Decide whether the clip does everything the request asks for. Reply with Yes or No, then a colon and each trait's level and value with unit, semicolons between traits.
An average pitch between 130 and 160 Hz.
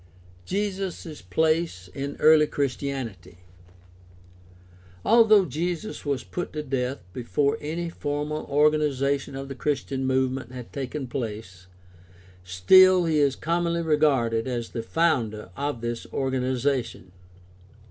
Yes: medium, 140 Hz